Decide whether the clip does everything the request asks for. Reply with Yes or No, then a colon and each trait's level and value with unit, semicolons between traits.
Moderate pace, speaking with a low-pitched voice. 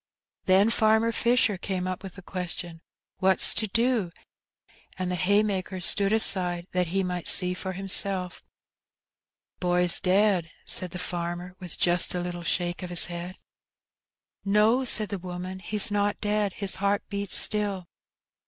No: average, 155 wpm; medium, 185 Hz